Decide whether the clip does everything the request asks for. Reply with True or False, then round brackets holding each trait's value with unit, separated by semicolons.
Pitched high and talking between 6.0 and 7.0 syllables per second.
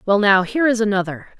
True (210 Hz; 6.8 syllables/s)